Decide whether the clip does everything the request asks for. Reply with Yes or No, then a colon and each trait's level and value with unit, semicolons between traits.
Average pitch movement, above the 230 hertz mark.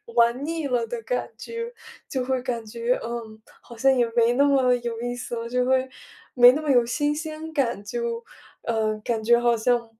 Yes: average, 3.2 semitones; high, 245 Hz